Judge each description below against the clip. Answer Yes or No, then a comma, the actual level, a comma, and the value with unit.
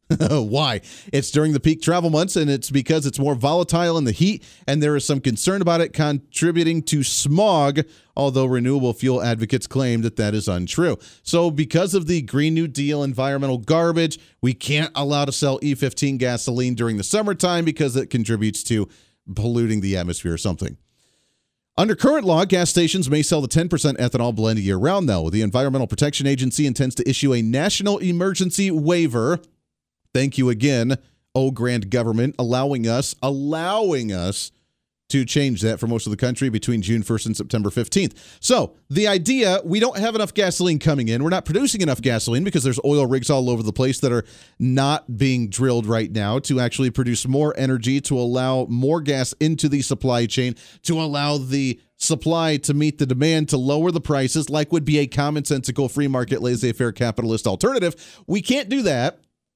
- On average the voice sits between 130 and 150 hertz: Yes, medium, 140 Hz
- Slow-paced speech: No, average, 180 wpm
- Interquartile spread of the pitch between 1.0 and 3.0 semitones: No, average, 4.6 semitones